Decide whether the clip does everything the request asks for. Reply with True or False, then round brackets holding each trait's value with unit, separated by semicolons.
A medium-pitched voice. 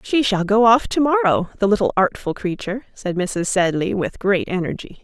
False (205 Hz)